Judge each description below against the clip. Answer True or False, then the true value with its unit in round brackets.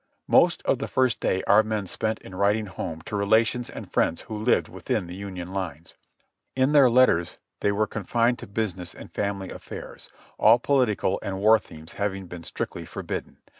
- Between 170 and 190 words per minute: True (180 wpm)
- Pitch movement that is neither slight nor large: True (3.2 semitones)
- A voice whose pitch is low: True (100 Hz)